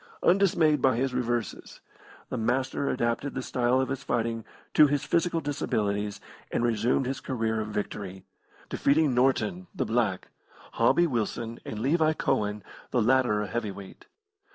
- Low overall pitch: Yes, low, 125 Hz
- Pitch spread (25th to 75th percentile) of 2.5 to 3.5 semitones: No, average, 4.0 semitones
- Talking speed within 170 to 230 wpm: No, average, 150 wpm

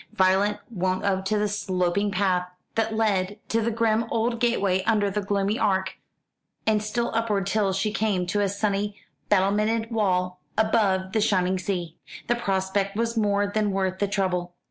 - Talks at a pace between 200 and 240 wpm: No, average, 165 wpm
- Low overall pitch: No, high, 200 Hz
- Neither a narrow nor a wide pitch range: No, narrow, 2.3 semitones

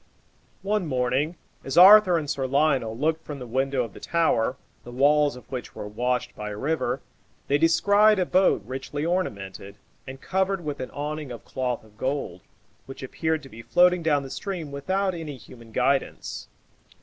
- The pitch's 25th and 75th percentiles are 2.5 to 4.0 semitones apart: No, average, 4.8 semitones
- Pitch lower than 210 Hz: Yes, medium, 140 Hz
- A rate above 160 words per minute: Yes, average, 175 wpm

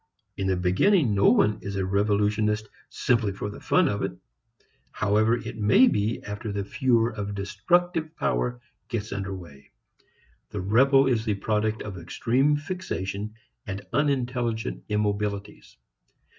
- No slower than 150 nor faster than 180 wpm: No, average, 140 wpm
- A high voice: No, low, 105 Hz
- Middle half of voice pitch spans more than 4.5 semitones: No, average, 3.4 semitones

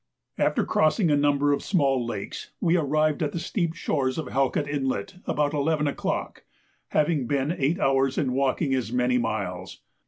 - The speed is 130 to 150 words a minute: No, average, 165 wpm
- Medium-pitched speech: Yes, medium, 145 Hz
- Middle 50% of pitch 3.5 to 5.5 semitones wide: No, average, 2.8 semitones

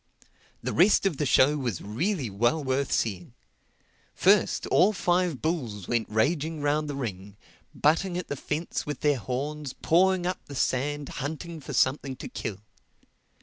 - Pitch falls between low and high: Yes, medium, 145 Hz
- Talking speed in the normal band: Yes, average, 155 wpm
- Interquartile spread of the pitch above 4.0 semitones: Yes, average, 4.8 semitones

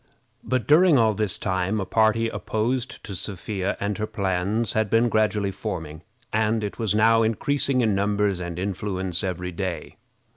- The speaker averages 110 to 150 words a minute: No, average, 160 wpm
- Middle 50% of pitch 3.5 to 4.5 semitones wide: No, average, 2.9 semitones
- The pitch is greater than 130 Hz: No, low, 105 Hz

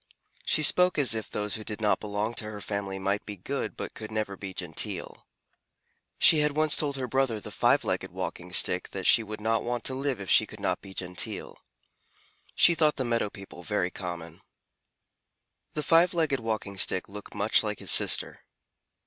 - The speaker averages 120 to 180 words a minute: No, average, 190 wpm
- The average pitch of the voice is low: Yes, low, 110 Hz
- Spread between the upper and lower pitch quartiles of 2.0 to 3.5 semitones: No, average, 5.2 semitones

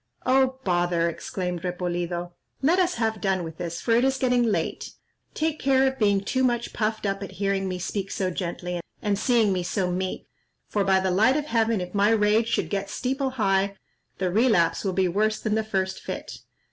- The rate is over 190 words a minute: Yes, average, 200 wpm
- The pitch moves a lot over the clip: No, average, 4.3 semitones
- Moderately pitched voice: No, high, 200 Hz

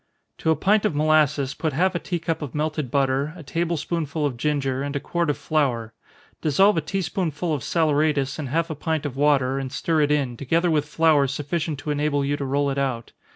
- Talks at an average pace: No, fast, 230 wpm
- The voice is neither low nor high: Yes, medium, 150 Hz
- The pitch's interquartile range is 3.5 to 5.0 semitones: No, narrow, 2.6 semitones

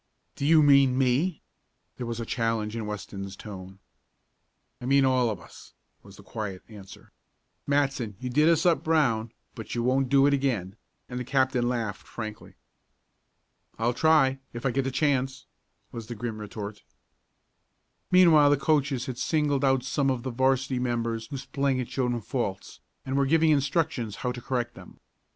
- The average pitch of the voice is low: Yes, low, 130 Hz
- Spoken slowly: No, average, 170 wpm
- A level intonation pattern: No, average, 3.3 semitones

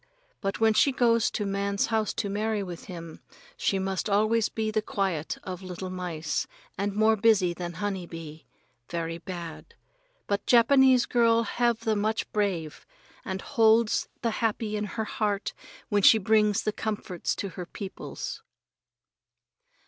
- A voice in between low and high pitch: No, high, 205 Hz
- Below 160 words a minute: Yes, average, 150 wpm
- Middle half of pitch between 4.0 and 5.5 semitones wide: No, average, 3.2 semitones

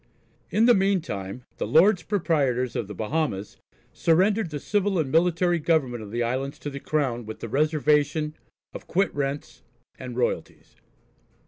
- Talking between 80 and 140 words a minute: No, average, 150 wpm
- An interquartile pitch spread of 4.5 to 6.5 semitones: Yes, wide, 5.6 semitones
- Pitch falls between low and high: Yes, medium, 150 Hz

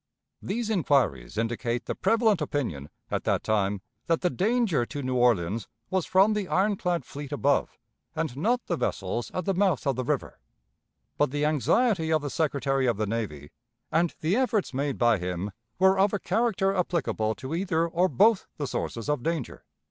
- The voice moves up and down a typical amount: No, wide, 7.9 semitones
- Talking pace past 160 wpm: Yes, average, 180 wpm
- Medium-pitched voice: Yes, medium, 150 Hz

